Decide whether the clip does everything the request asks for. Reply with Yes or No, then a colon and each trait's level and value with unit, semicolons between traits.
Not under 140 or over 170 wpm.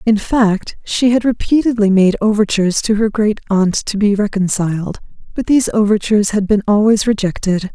Yes: average, 165 wpm